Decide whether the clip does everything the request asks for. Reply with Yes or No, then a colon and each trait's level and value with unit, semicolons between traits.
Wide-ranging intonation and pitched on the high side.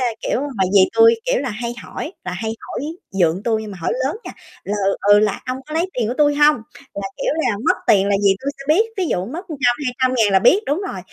Yes: wide, 6.6 semitones; high, 245 Hz